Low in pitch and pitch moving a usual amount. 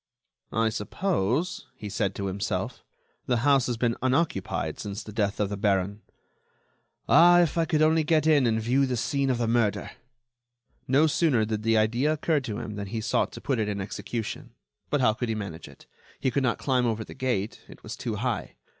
Yes: low, 120 Hz; average, 4.8 semitones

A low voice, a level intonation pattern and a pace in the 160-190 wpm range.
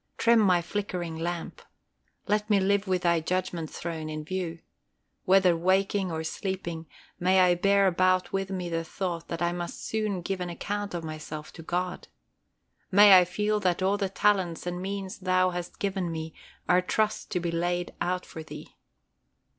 No: medium, 180 Hz; narrow, 2.2 semitones; average, 175 wpm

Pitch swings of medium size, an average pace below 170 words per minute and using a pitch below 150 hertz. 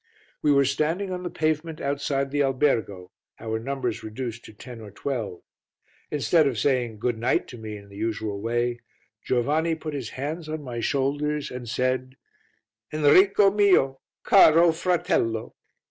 Yes: average, 4.9 semitones; average, 150 wpm; low, 135 Hz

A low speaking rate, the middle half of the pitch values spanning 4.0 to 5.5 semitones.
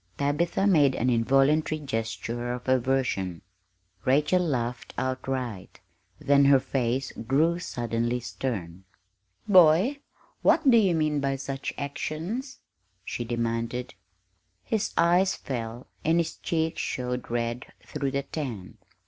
Yes: slow, 115 wpm; average, 4.7 semitones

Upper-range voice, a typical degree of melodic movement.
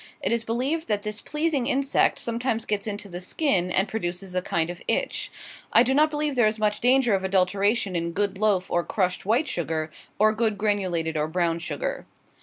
Yes: high, 210 Hz; average, 4.8 semitones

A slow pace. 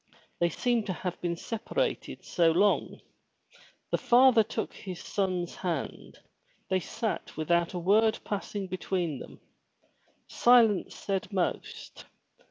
Yes: slow, 120 wpm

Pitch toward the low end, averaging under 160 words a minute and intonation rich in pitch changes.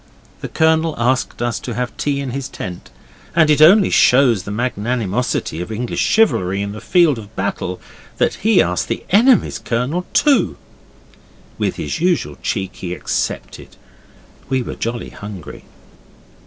Yes: low, 125 Hz; average, 150 wpm; wide, 7.4 semitones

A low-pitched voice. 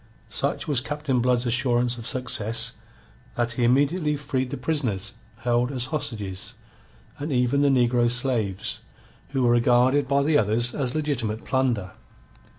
Yes: low, 125 Hz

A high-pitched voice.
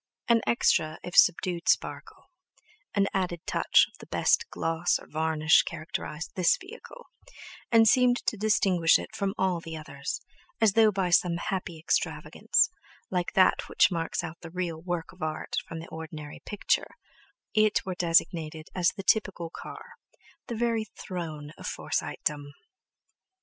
No: medium, 175 Hz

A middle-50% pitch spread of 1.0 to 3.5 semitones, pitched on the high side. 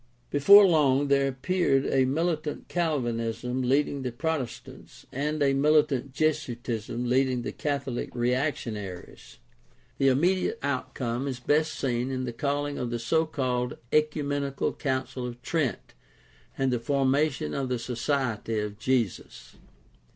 No: average, 3.0 semitones; low, 135 Hz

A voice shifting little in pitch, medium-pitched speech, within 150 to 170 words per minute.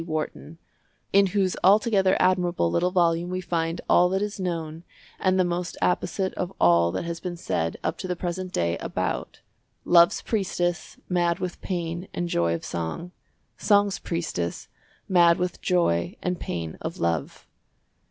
Yes: narrow, 2.3 semitones; medium, 175 Hz; average, 155 wpm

